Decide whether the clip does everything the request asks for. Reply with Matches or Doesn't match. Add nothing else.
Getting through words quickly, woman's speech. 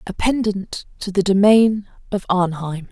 Doesn't match